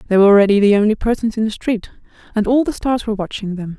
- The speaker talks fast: Yes, fast, 255 wpm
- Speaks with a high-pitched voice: Yes, high, 215 Hz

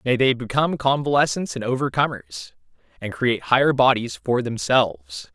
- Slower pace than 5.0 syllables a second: No, 5.2 syllables/s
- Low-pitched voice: Yes, low, 120 Hz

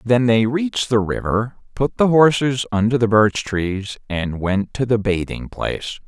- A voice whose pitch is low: Yes, low, 115 Hz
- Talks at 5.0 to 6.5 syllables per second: No, 4.3 syllables/s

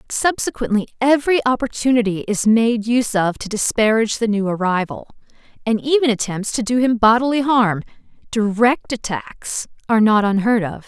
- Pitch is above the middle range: Yes, high, 225 Hz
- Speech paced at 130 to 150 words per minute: Yes, average, 145 wpm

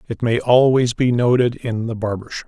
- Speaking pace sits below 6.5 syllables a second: Yes, 5.0 syllables/s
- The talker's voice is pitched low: Yes, low, 120 Hz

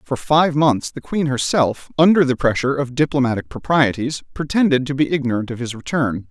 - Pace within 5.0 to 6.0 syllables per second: Yes, 5.5 syllables/s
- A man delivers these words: Yes, male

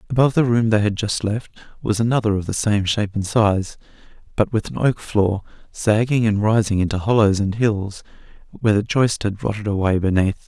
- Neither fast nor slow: Yes, average, 195 wpm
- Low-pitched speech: Yes, low, 105 Hz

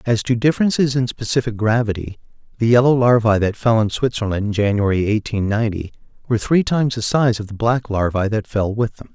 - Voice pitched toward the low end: Yes, low, 115 Hz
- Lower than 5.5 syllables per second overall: No, 5.8 syllables/s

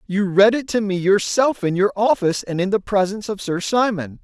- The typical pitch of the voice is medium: No, high, 200 Hz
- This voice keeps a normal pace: No, fast, 225 wpm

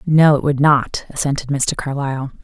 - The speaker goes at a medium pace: Yes, average, 170 wpm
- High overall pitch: No, medium, 140 Hz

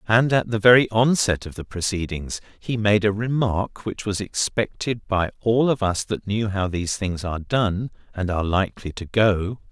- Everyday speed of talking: Yes, average, 190 wpm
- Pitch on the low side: Yes, low, 105 Hz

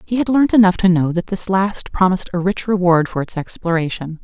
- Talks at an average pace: No, fast, 225 wpm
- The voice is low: No, medium, 185 Hz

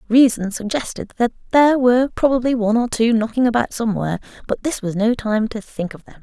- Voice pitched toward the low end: No, high, 230 Hz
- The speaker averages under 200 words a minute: No, fast, 205 wpm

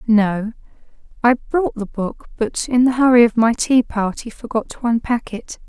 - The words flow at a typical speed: Yes, average, 180 wpm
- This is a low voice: No, high, 235 Hz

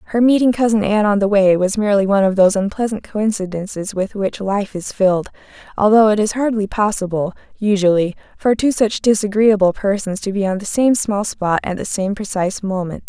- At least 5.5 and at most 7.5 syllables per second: Yes, 5.6 syllables/s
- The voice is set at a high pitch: Yes, high, 205 Hz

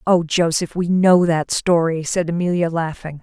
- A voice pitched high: No, medium, 170 Hz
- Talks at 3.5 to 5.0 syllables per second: Yes, 4.5 syllables/s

